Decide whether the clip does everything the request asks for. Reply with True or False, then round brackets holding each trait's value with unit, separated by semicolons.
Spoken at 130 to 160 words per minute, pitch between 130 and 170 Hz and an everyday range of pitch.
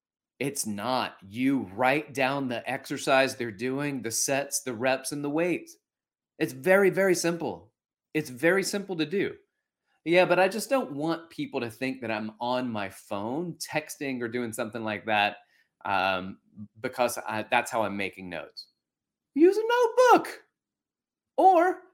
False (155 wpm; 140 Hz; 7.9 semitones)